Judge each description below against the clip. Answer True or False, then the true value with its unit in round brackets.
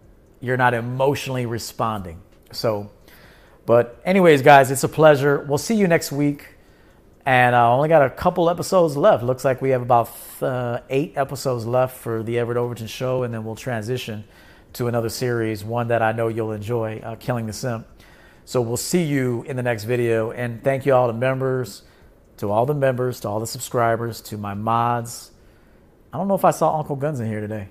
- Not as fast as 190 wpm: False (200 wpm)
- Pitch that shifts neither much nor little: True (3.0 semitones)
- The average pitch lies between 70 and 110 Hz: False (120 Hz)